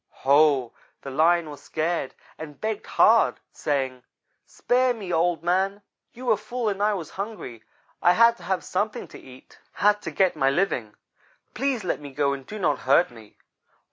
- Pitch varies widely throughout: Yes, wide, 6.7 semitones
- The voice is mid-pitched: Yes, medium, 175 Hz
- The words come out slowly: No, average, 175 wpm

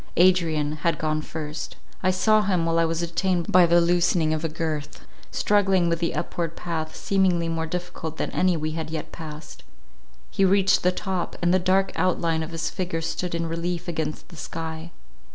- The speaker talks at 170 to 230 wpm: Yes, average, 190 wpm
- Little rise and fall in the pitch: Yes, narrow, 2.1 semitones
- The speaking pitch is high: No, medium, 170 Hz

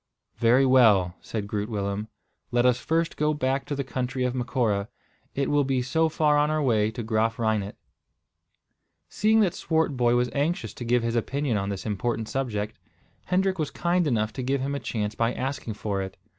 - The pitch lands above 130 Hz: No, low, 125 Hz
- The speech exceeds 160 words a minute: Yes, average, 190 wpm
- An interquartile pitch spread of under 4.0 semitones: No, average, 4.5 semitones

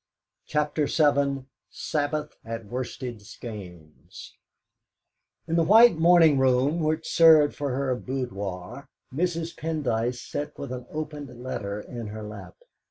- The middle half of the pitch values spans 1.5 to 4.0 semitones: No, average, 4.8 semitones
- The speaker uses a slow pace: Yes, slow, 120 wpm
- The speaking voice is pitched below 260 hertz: Yes, medium, 140 Hz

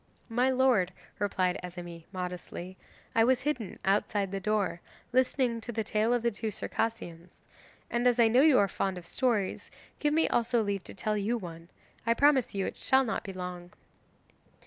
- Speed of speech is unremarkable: Yes, average, 180 wpm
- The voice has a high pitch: Yes, high, 215 Hz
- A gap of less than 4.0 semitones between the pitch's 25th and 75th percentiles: No, average, 4.7 semitones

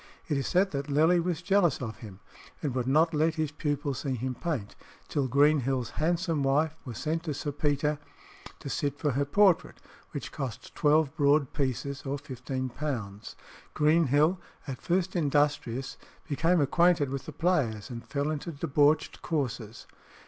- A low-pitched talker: No, medium, 145 Hz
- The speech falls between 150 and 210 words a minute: Yes, average, 155 wpm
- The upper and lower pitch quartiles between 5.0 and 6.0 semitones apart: No, average, 3.0 semitones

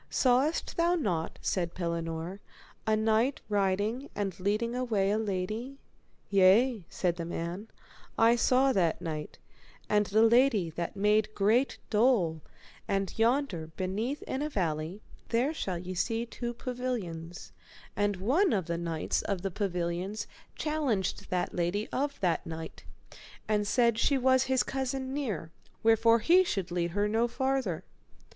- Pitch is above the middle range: Yes, high, 210 Hz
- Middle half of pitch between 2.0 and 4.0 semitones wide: No, wide, 5.6 semitones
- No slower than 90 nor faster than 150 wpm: Yes, average, 145 wpm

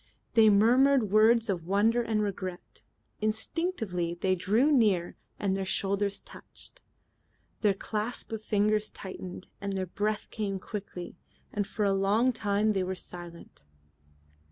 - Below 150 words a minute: Yes, slow, 135 wpm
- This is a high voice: Yes, high, 205 Hz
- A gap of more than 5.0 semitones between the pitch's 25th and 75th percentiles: No, narrow, 2.5 semitones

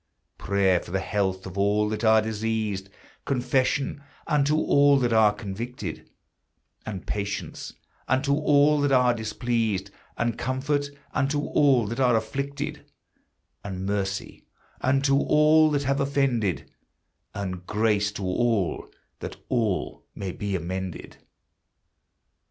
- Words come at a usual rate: No, slow, 120 wpm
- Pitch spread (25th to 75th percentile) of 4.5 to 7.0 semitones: Yes, wide, 5.5 semitones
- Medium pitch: No, low, 115 Hz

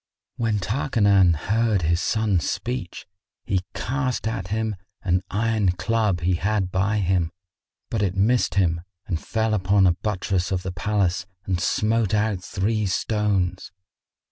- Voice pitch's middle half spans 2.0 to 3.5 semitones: Yes, average, 3.2 semitones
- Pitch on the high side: No, low, 100 Hz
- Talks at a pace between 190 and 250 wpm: No, average, 140 wpm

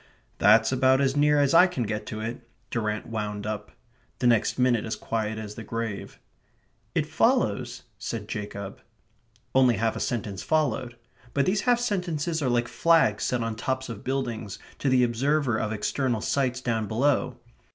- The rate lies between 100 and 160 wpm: No, average, 170 wpm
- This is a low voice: Yes, low, 120 Hz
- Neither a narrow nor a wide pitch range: Yes, average, 3.8 semitones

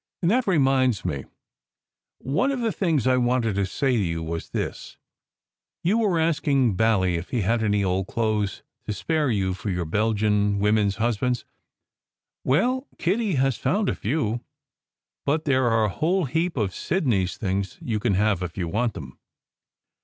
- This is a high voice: No, low, 115 Hz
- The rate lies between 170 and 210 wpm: Yes, average, 175 wpm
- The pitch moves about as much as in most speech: No, wide, 6.9 semitones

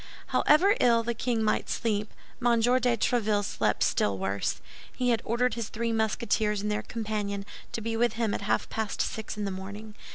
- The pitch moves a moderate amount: No, narrow, 2.1 semitones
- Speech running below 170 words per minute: No, average, 190 wpm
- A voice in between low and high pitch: No, high, 220 Hz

